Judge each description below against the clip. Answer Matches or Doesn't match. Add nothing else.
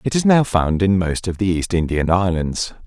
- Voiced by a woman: Doesn't match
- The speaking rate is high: Matches